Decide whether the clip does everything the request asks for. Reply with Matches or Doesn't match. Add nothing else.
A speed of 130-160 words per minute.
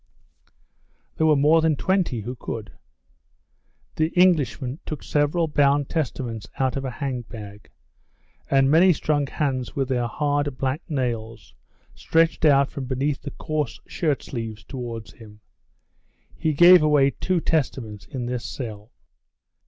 Matches